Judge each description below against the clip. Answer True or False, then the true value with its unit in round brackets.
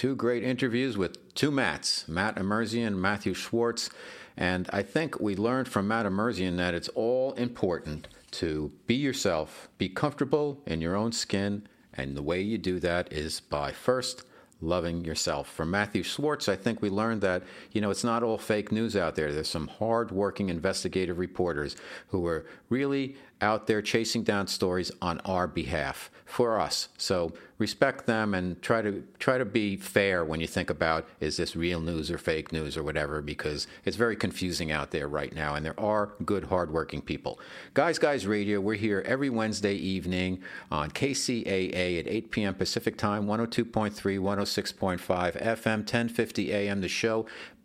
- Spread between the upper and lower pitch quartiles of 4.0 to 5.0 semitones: True (4.4 semitones)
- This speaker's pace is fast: False (175 wpm)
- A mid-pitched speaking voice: False (100 Hz)